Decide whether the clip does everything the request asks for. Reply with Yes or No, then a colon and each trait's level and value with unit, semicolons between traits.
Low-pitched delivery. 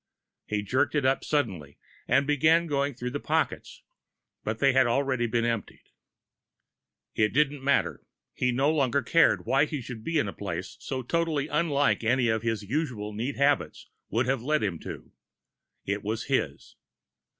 Yes: low, 130 Hz